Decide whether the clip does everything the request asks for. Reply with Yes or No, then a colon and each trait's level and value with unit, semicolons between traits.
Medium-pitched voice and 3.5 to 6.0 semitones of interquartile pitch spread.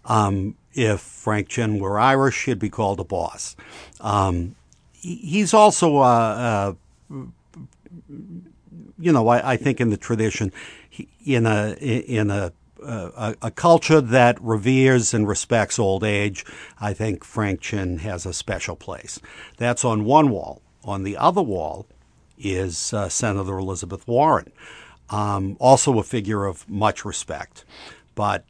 No: low, 110 Hz; average, 4.1 semitones